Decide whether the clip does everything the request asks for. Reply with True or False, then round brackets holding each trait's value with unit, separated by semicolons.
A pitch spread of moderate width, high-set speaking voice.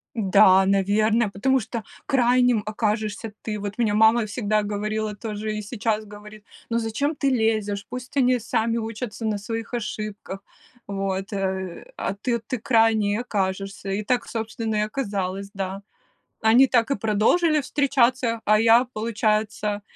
False (2.3 semitones; 215 Hz)